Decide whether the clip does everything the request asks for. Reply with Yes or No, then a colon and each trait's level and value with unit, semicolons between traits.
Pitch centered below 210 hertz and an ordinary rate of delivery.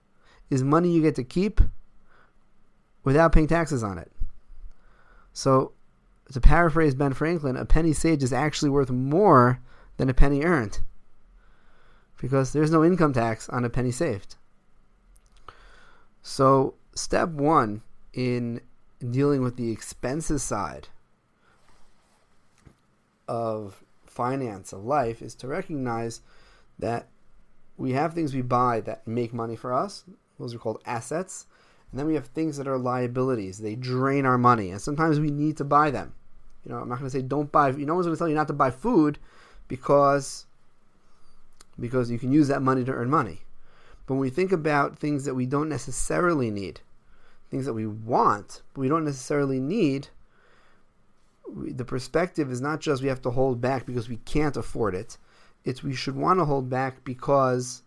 Yes: low, 135 Hz; average, 165 wpm